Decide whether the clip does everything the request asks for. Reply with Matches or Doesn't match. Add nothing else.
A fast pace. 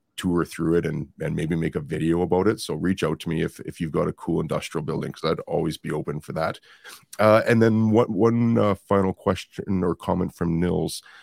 Matches